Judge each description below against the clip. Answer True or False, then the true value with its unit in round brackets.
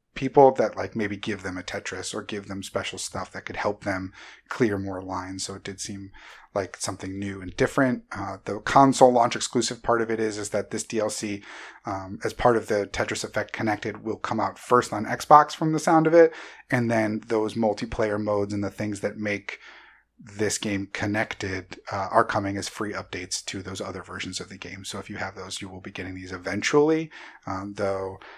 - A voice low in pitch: True (105 Hz)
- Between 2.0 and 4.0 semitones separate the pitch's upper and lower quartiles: True (2.9 semitones)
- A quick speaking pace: True (210 wpm)